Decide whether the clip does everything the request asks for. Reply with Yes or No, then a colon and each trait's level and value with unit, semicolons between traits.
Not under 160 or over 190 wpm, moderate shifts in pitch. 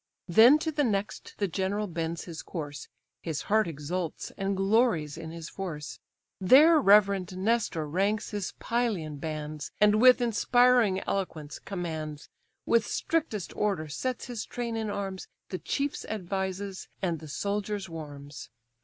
No: average, 140 wpm; average, 5.0 semitones